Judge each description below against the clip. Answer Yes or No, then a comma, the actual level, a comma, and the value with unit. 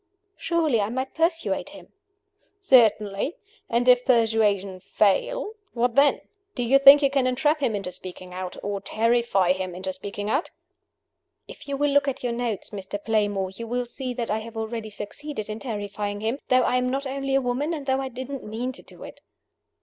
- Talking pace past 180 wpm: Yes, average, 190 wpm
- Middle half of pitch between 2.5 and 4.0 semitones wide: No, average, 4.7 semitones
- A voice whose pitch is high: Yes, high, 235 Hz